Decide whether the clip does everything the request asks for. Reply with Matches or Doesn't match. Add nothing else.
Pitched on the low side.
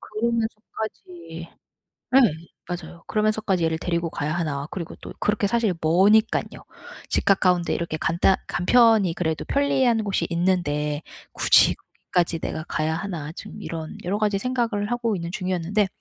Doesn't match